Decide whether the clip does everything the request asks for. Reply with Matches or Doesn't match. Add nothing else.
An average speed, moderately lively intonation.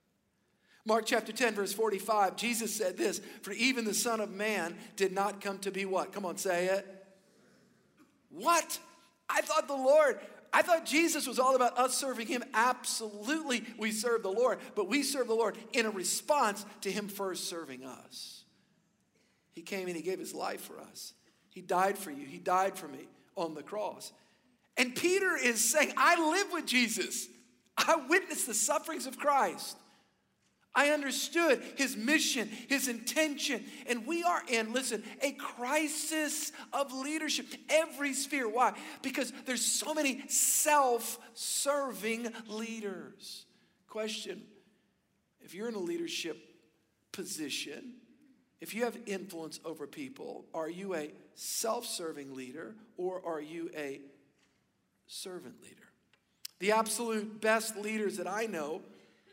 Doesn't match